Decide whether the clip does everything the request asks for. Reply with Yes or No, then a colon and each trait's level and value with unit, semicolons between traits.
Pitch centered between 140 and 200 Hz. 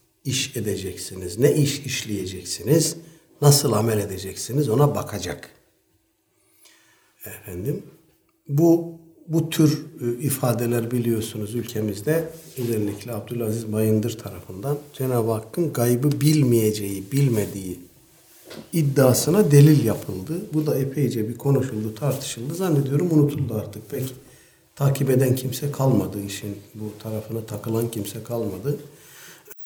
No: low, 125 Hz